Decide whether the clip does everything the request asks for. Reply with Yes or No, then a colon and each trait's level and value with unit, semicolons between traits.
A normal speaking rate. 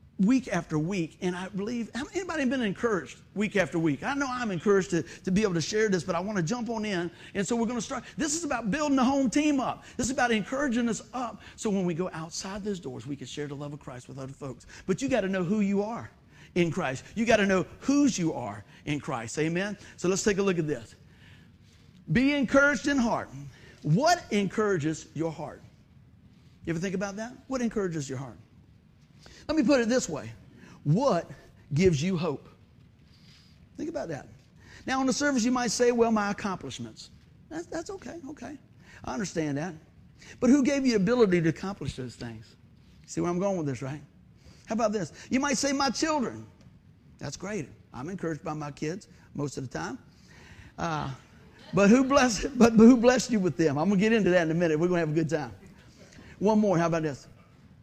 No: fast, 215 wpm